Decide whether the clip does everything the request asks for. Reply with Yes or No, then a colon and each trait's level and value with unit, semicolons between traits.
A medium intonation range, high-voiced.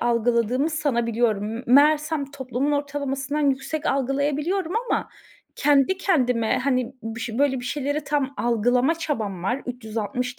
Yes: average, 3.4 semitones; very high, 265 Hz